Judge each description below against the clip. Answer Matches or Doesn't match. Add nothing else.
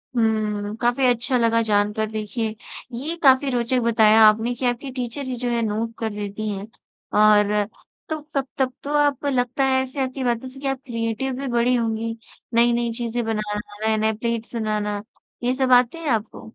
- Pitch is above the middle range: Matches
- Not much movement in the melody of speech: Doesn't match